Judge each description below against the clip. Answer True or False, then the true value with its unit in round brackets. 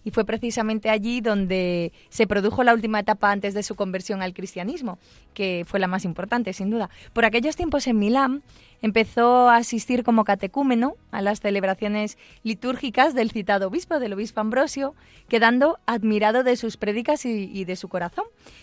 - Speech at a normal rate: True (165 wpm)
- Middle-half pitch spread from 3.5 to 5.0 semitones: False (3.1 semitones)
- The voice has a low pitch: False (220 Hz)